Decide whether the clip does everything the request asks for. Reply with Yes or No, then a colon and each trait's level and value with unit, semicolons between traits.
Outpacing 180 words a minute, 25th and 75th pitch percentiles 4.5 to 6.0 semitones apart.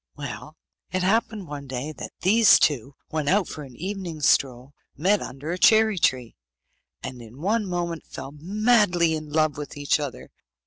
No: average, 170 wpm; average, 5.3 semitones